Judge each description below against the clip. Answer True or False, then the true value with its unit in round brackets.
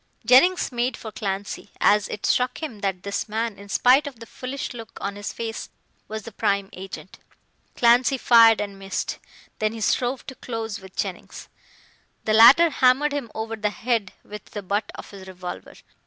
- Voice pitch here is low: False (220 Hz)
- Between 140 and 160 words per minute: False (180 wpm)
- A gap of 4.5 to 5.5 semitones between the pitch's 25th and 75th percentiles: False (3.6 semitones)